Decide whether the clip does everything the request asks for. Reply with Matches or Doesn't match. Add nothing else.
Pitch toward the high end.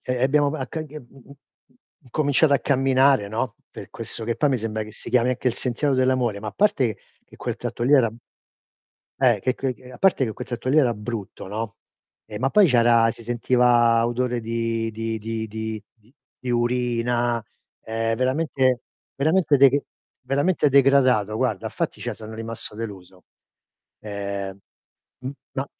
Doesn't match